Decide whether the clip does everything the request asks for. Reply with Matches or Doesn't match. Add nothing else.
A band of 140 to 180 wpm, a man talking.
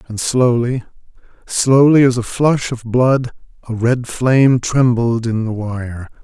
Matches